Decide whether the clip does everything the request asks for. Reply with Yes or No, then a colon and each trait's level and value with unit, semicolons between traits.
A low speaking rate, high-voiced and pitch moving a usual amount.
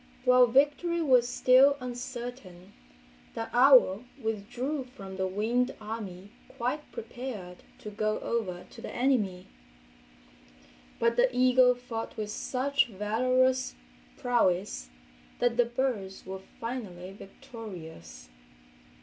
Yes: slow, 105 wpm; high, 235 Hz; average, 4.3 semitones